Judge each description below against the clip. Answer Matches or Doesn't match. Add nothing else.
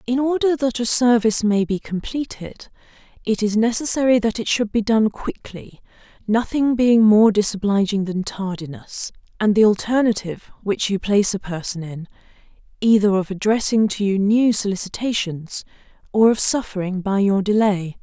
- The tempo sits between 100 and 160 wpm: Matches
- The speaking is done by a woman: Matches